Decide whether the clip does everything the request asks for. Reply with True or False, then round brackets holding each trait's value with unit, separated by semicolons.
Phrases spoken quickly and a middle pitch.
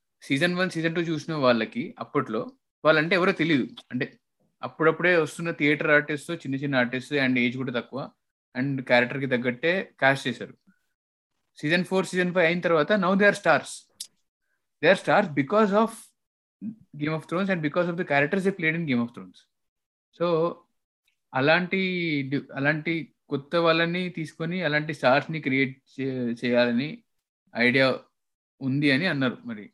True (145 wpm; 155 Hz)